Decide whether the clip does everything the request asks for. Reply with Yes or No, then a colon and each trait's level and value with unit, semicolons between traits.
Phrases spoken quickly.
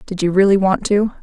Yes: fast, 245 wpm